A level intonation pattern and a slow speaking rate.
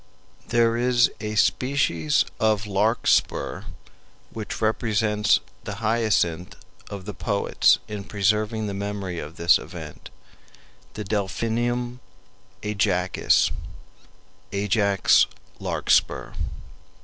Yes: narrow, 2.2 semitones; slow, 90 wpm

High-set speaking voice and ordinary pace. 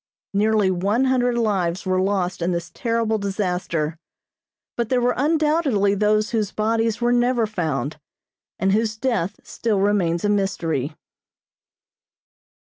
No: high, 205 Hz; slow, 125 wpm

